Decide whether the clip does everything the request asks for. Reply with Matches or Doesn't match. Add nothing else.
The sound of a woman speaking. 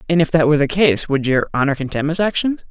Doesn't match